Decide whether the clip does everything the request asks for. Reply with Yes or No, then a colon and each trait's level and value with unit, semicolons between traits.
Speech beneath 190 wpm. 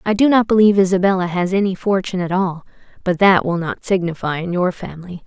No: fast, 205 wpm